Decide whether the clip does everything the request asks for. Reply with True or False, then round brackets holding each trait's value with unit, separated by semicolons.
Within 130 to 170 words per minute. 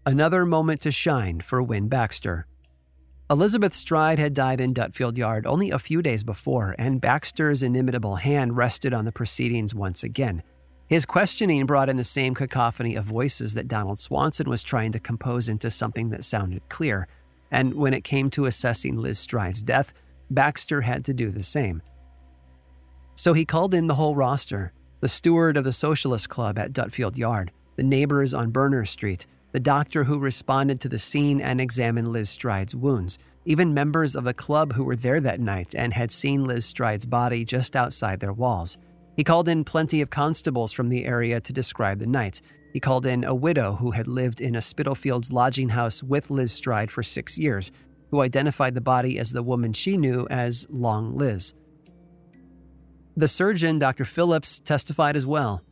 False (180 wpm)